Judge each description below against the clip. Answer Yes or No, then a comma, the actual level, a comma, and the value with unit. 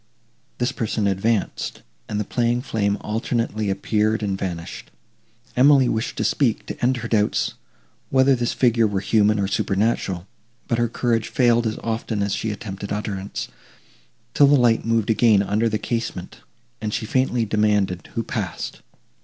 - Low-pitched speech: Yes, low, 110 Hz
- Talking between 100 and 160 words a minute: Yes, average, 155 wpm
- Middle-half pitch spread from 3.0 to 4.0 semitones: No, narrow, 2.6 semitones